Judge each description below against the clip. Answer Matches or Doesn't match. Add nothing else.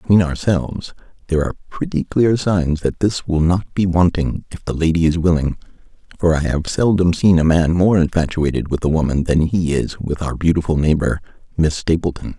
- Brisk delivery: Doesn't match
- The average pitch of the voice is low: Matches